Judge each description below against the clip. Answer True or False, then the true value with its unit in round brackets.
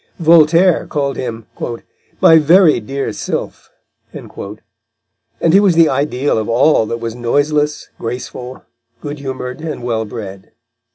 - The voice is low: True (130 Hz)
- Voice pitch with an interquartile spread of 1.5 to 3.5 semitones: False (5.1 semitones)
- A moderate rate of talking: False (125 wpm)